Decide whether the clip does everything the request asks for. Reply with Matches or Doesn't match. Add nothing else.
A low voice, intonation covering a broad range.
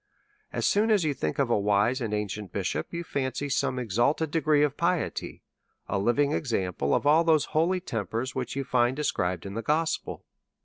Matches